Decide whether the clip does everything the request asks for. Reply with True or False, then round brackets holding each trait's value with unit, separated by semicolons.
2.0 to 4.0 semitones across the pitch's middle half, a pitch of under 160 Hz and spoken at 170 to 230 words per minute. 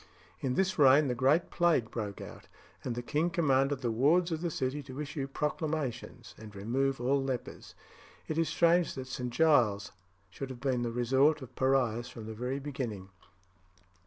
True (3.7 semitones; 135 Hz; 175 wpm)